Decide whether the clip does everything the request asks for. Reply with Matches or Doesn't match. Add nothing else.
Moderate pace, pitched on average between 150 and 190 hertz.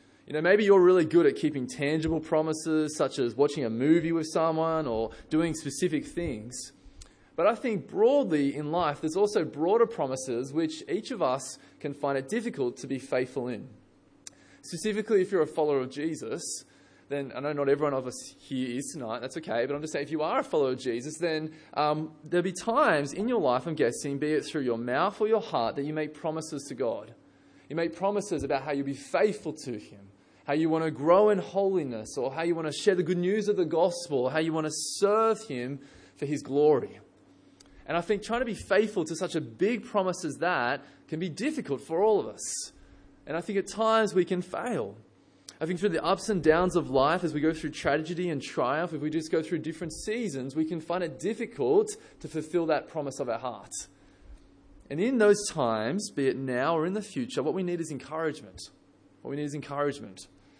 Doesn't match